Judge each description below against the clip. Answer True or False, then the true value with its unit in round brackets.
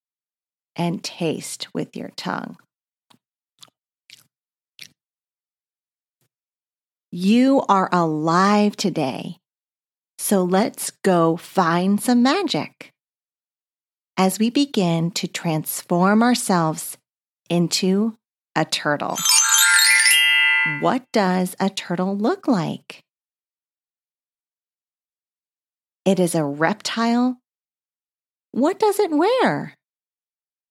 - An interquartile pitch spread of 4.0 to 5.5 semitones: True (5.0 semitones)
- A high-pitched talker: True (195 Hz)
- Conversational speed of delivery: False (75 wpm)